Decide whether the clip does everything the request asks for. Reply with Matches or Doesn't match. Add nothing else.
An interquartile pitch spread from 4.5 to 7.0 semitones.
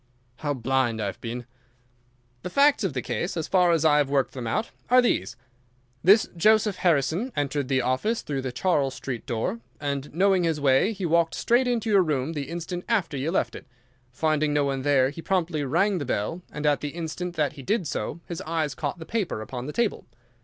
Matches